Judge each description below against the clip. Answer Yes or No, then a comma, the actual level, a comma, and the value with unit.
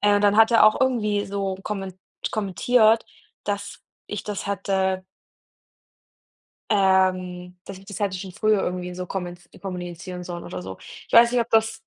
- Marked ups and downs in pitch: No, narrow, 2.6 semitones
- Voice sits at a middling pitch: No, high, 195 Hz